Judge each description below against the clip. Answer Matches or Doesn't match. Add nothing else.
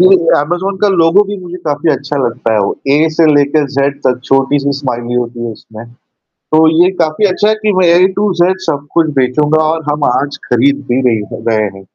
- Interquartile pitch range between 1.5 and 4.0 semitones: Doesn't match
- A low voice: Doesn't match